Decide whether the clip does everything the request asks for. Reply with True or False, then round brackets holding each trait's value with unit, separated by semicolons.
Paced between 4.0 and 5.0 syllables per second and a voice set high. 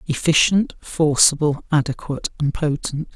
False (4.7 syllables/s; 150 Hz)